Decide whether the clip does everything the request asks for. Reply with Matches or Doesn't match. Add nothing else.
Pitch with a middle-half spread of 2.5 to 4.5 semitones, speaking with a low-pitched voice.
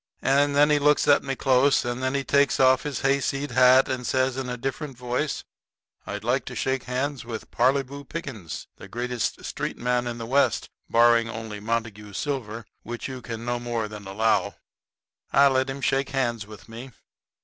Matches